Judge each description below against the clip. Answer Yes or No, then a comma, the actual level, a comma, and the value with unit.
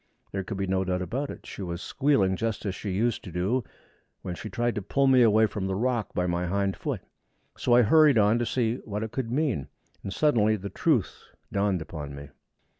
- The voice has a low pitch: Yes, low, 105 Hz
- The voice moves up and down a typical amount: Yes, average, 4.2 semitones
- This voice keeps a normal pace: No, fast, 220 wpm